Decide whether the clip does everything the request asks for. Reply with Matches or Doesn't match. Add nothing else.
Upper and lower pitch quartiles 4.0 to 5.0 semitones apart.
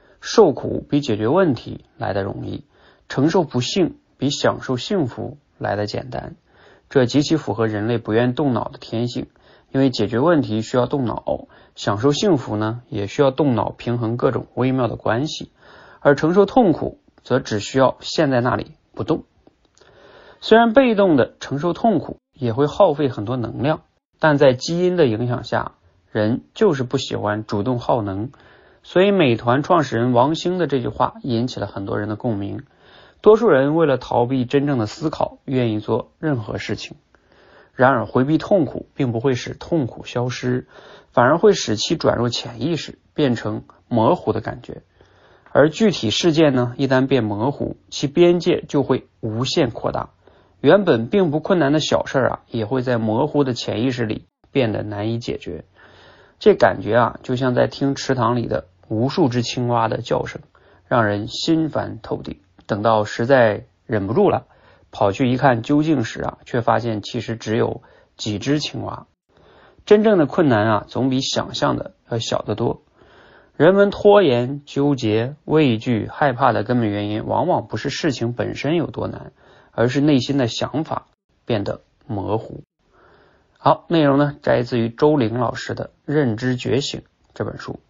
Matches